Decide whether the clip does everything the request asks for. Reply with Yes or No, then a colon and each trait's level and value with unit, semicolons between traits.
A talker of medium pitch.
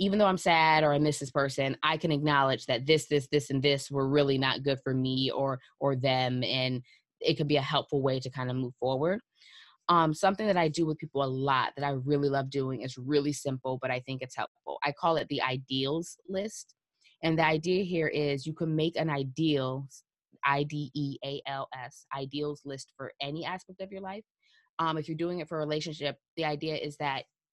Yes: medium, 145 Hz